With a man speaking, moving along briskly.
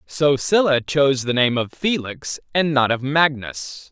No: male; average, 170 wpm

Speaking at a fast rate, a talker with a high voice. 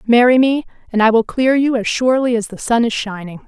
Yes: fast, 240 wpm; high, 235 Hz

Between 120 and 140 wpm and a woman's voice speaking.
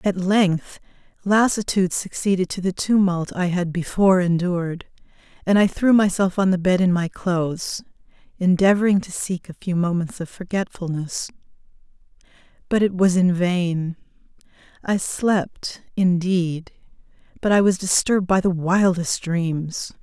Yes: slow, 135 wpm; female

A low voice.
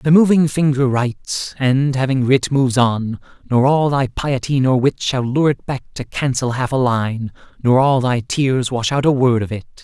Yes: low, 130 Hz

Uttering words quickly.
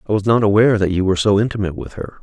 Yes: fast, 295 wpm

